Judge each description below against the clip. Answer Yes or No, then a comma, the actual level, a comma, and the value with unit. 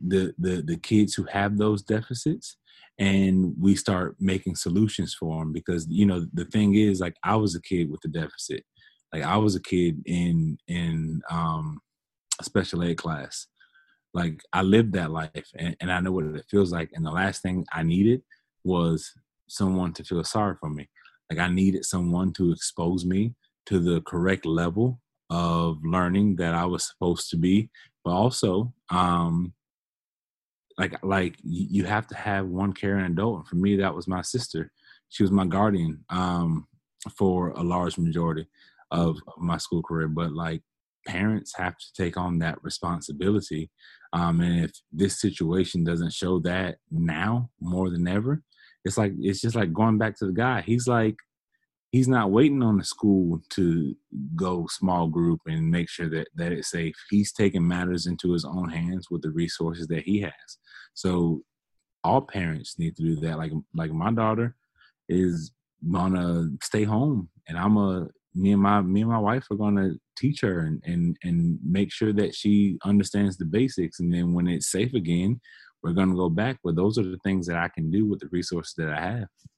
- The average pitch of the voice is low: Yes, very low, 90 Hz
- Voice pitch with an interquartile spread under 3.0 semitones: No, average, 3.3 semitones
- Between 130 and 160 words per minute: No, average, 185 wpm